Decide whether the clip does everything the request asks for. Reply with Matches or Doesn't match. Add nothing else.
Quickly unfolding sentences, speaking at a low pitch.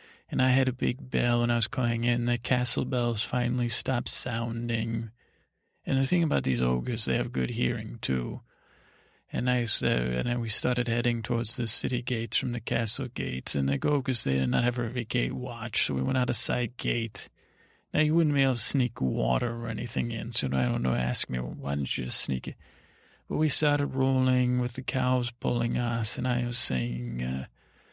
Matches